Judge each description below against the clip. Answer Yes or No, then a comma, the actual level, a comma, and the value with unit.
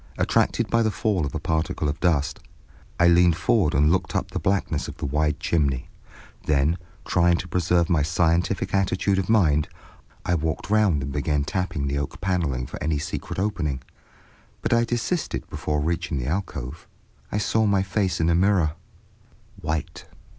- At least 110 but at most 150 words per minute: No, average, 170 wpm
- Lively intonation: No, average, 4.1 semitones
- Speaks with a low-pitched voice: Yes, very low, 85 Hz